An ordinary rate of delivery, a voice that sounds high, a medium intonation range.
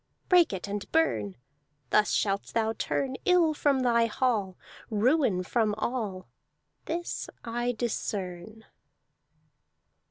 No: slow, 105 wpm; high, 225 Hz; average, 4.5 semitones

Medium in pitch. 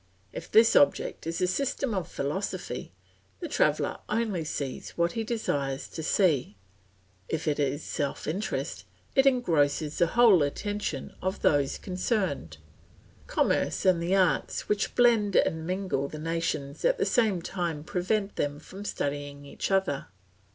Yes: medium, 170 Hz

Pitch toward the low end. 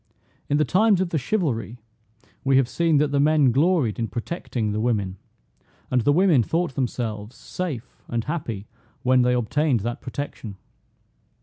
Yes: low, 130 Hz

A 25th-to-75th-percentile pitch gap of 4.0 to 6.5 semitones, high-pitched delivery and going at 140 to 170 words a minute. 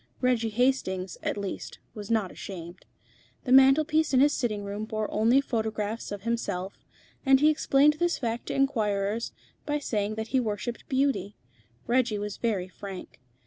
Yes: average, 4.6 semitones; high, 225 Hz; average, 160 wpm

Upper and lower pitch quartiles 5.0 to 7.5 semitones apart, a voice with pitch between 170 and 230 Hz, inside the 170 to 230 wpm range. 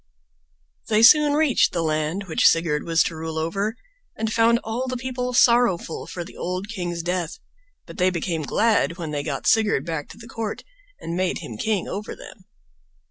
Yes: wide, 5.5 semitones; medium, 185 Hz; average, 185 wpm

